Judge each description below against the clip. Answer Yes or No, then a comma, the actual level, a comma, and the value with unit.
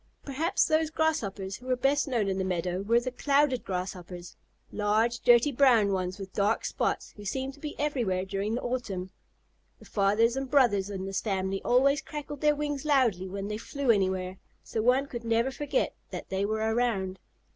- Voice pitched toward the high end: Yes, high, 230 Hz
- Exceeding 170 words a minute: Yes, average, 185 wpm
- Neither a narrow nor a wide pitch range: No, wide, 5.7 semitones